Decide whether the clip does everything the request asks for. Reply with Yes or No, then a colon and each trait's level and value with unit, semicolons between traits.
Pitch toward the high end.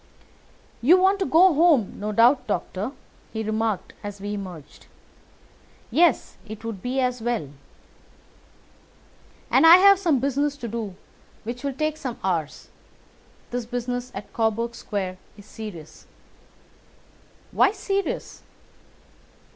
Yes: high, 235 Hz